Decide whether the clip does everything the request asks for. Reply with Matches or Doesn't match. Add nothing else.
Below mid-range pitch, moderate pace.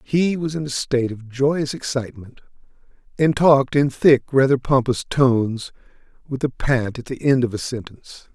Matches